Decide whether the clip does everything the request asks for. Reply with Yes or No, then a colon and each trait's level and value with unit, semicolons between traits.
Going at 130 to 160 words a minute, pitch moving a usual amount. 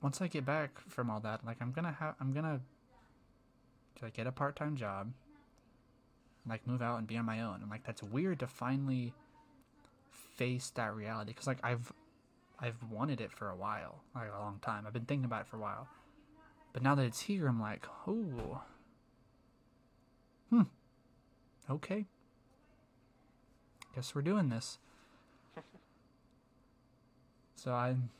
No: average, 155 wpm; narrow, 1.9 semitones